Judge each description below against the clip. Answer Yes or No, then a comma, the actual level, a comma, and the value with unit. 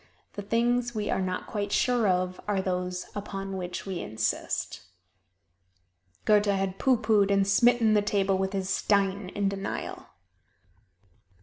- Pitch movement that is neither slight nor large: No, narrow, 1.8 semitones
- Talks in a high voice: Yes, high, 200 Hz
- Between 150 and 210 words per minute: No, average, 140 wpm